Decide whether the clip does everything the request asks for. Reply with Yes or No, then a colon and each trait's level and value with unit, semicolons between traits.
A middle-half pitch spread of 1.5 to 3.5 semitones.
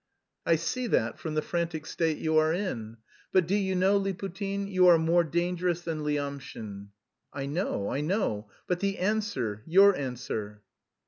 No: average, 5.2 semitones